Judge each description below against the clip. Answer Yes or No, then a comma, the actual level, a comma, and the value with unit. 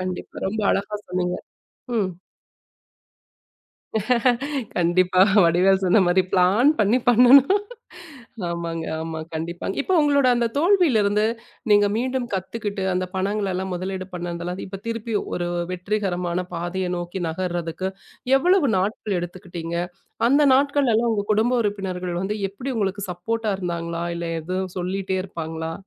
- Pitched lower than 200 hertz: Yes, high, 190 Hz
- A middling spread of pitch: Yes, average, 3.6 semitones